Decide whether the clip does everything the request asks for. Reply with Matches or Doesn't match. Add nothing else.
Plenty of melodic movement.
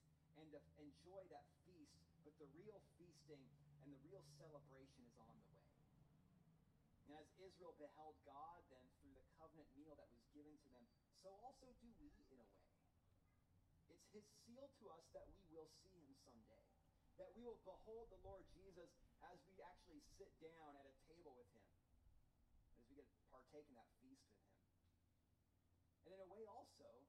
Matches